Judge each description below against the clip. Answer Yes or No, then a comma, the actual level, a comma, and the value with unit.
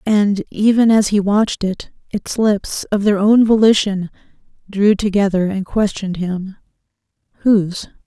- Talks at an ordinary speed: No, slow, 125 wpm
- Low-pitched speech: No, high, 200 Hz